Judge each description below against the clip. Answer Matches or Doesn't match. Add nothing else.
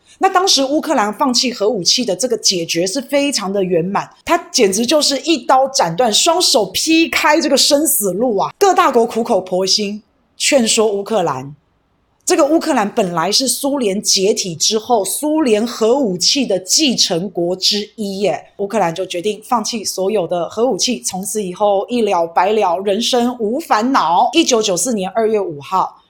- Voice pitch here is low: Doesn't match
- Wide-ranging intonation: Matches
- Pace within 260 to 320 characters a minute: Matches